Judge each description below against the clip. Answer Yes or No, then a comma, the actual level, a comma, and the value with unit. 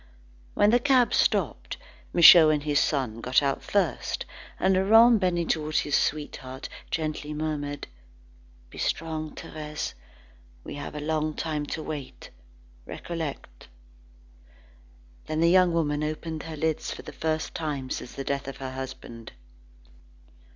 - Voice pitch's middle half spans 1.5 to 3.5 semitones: Yes, narrow, 2.4 semitones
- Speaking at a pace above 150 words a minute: No, average, 140 wpm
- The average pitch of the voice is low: No, medium, 155 Hz